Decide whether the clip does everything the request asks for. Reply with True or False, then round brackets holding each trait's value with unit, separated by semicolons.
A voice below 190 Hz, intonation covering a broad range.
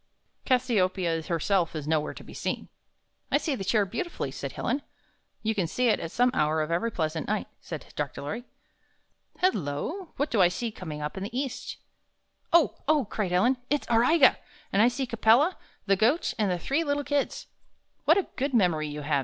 False (215 Hz; 7.9 semitones)